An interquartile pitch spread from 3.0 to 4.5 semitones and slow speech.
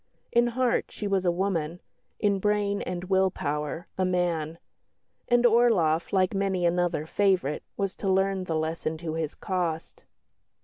No: average, 3.3 semitones; average, 150 wpm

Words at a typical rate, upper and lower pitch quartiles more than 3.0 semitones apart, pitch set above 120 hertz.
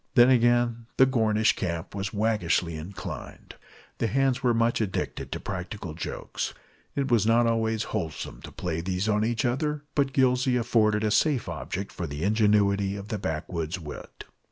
No: average, 165 wpm; average, 4.2 semitones; low, 110 Hz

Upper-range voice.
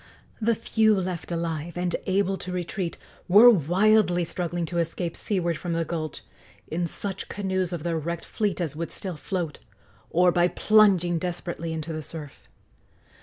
No: medium, 175 Hz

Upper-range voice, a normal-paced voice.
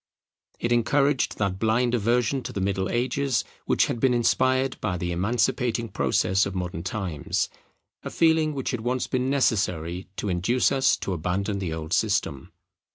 No: low, 110 Hz; average, 160 wpm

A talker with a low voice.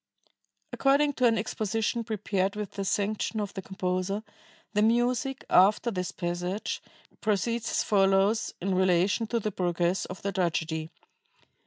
No: high, 200 Hz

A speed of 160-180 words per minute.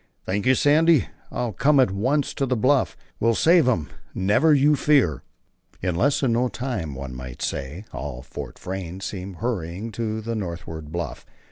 Yes: average, 170 wpm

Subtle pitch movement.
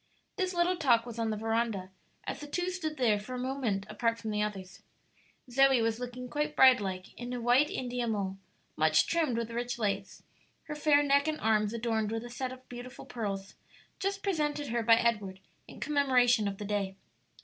No: average, 4.3 semitones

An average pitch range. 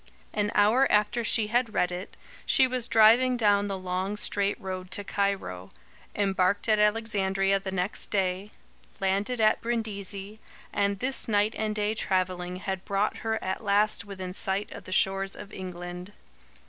No: narrow, 2.1 semitones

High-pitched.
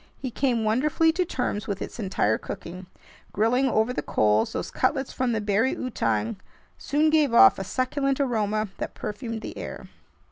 Yes: high, 230 Hz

